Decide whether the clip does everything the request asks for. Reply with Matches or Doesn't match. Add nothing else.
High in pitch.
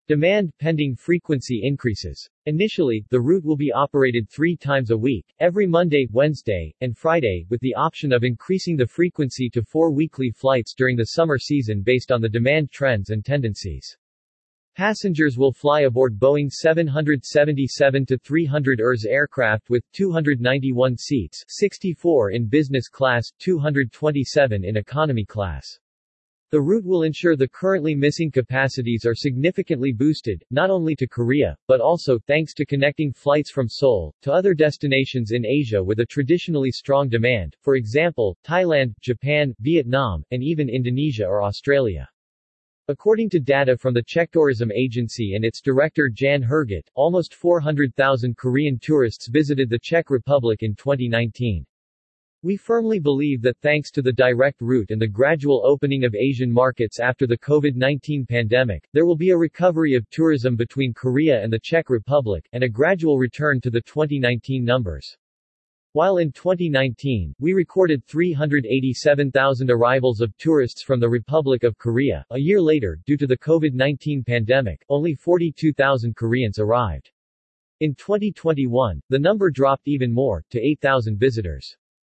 Doesn't match